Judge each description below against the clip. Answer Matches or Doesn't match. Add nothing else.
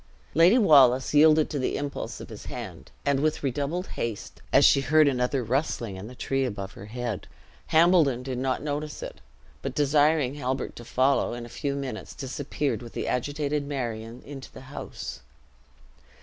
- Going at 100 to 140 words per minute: Doesn't match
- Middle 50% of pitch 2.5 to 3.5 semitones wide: Matches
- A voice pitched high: Doesn't match